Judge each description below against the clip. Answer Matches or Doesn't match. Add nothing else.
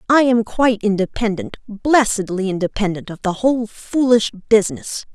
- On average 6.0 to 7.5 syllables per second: Doesn't match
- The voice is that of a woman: Matches